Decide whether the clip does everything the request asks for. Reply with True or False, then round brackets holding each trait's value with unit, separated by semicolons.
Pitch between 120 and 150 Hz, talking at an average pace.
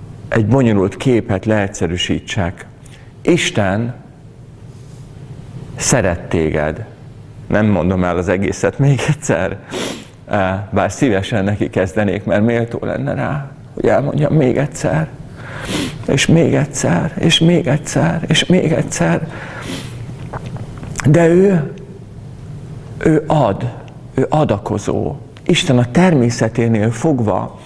False (130 Hz; 100 wpm)